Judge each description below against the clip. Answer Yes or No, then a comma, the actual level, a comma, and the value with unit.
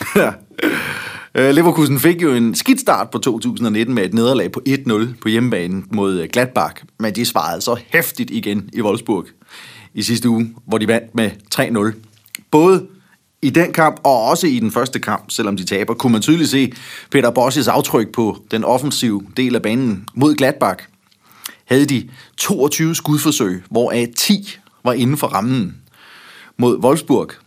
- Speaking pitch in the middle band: No, low, 125 Hz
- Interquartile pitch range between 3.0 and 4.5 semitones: No, wide, 5.6 semitones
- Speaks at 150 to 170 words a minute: Yes, average, 160 wpm